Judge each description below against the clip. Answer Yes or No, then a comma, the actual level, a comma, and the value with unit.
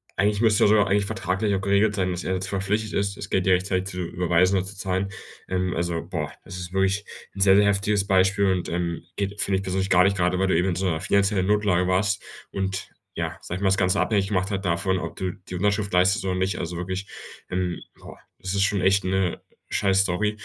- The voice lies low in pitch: Yes, very low, 95 Hz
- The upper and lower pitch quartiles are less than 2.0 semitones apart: Yes, narrow, 1.6 semitones